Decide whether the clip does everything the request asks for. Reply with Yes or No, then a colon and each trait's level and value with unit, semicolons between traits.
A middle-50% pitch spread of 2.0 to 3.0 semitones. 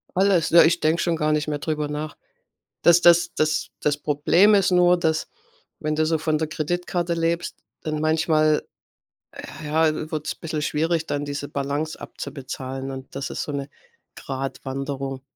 Yes: narrow, 2.4 semitones